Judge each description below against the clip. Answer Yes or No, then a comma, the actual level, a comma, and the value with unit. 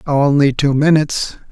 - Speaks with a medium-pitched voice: Yes, medium, 145 Hz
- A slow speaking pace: Yes, slow, 120 wpm